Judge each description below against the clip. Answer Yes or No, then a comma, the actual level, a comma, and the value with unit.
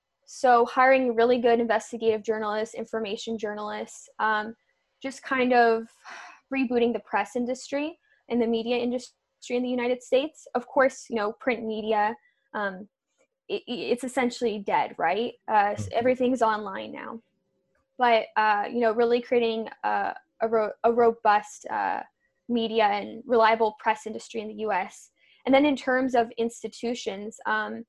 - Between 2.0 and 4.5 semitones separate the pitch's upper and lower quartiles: Yes, narrow, 2.6 semitones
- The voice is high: Yes, high, 235 Hz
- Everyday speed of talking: Yes, average, 145 wpm